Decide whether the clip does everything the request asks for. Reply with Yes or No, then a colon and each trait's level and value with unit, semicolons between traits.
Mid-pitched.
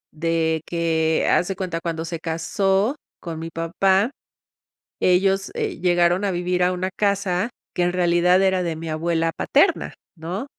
Yes: medium, 175 Hz